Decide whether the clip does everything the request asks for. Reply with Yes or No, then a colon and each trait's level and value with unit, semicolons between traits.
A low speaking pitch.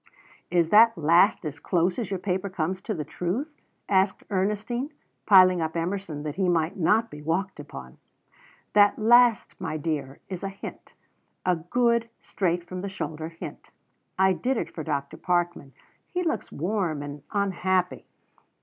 No: medium, 185 Hz